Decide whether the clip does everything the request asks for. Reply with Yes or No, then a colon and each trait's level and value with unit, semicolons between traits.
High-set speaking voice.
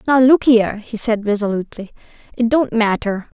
Yes: high, 225 Hz